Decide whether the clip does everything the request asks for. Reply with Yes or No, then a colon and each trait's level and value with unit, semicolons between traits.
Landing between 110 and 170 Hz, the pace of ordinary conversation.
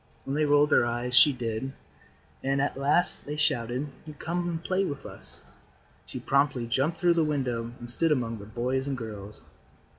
Yes: low, 135 Hz; average, 180 wpm